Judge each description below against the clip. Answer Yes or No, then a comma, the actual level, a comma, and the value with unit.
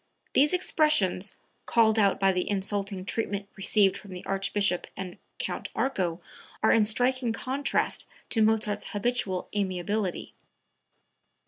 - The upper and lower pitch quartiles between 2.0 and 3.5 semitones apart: Yes, average, 2.9 semitones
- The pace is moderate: No, slow, 120 wpm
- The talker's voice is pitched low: No, high, 205 Hz